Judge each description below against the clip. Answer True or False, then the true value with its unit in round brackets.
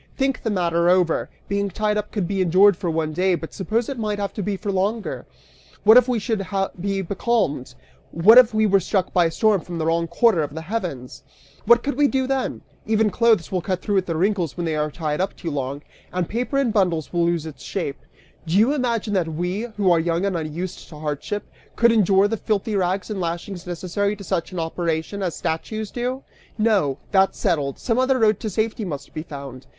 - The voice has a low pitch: False (190 Hz)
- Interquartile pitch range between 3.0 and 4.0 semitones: False (4.5 semitones)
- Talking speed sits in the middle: False (220 wpm)